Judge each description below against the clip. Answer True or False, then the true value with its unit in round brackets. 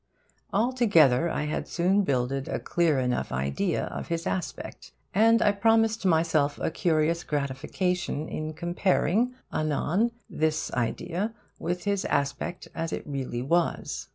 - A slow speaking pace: True (130 wpm)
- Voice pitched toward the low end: False (165 Hz)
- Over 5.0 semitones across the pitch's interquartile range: True (5.4 semitones)